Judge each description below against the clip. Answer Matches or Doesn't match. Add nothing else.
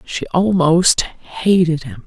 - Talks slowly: Matches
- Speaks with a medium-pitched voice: Matches